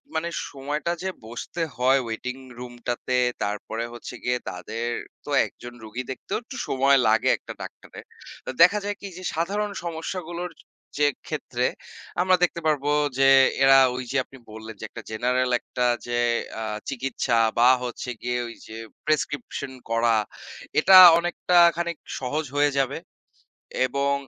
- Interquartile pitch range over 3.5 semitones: Yes, wide, 5.6 semitones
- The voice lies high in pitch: No, low, 135 Hz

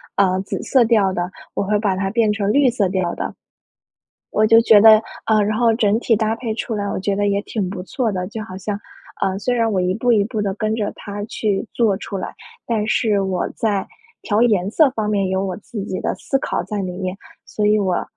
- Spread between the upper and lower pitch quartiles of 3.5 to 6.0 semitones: No, narrow, 2.4 semitones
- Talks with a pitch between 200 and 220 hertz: Yes, high, 210 Hz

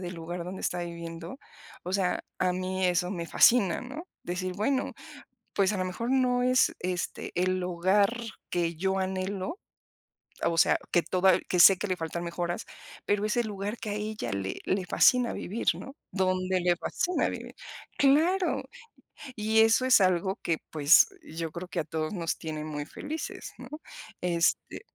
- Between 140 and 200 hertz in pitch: Yes, medium, 185 Hz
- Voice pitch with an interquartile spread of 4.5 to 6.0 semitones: No, average, 3.4 semitones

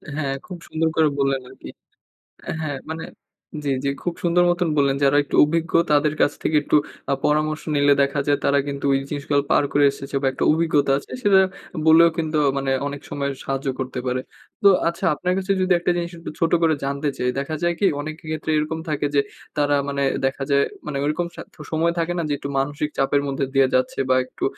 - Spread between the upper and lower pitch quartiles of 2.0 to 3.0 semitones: Yes, narrow, 2.6 semitones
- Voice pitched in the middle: Yes, medium, 145 Hz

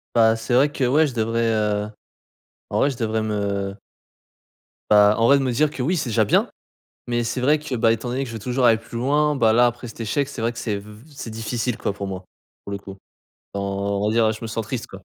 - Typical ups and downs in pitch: Yes, average, 3.0 semitones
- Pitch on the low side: Yes, low, 115 Hz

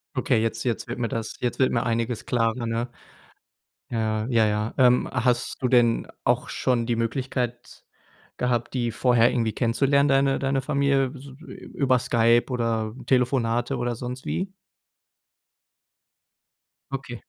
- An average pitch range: No, narrow, 2.1 semitones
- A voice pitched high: No, low, 120 Hz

